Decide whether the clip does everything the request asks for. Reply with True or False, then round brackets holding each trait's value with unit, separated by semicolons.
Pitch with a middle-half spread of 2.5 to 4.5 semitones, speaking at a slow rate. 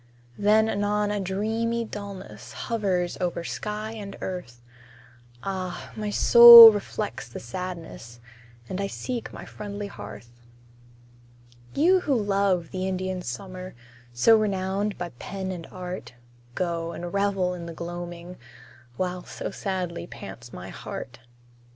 True (2.9 semitones; 125 wpm)